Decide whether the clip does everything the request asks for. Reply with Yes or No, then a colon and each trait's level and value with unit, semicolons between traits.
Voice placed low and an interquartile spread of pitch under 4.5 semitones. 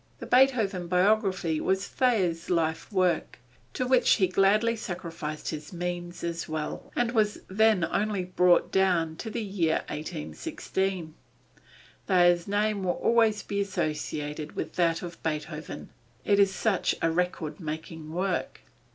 No: medium, 180 Hz; average, 3.7 semitones